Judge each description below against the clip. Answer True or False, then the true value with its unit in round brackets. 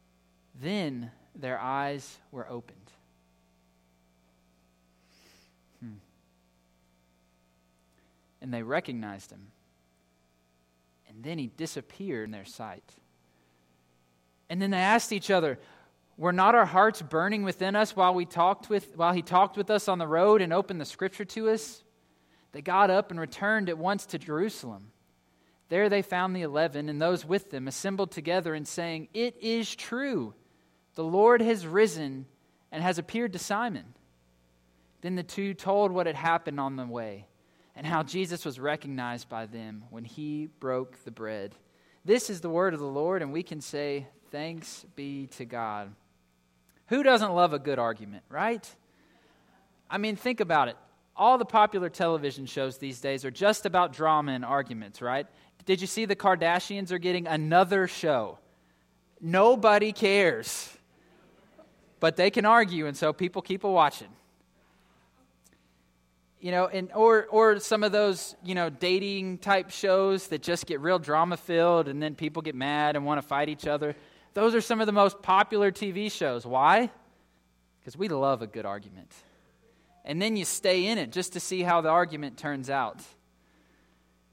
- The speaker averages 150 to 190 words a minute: True (160 wpm)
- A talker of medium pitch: True (155 Hz)